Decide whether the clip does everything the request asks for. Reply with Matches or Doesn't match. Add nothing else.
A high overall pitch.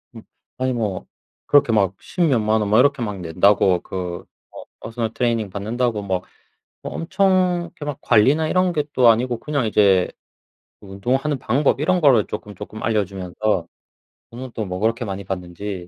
Doesn't match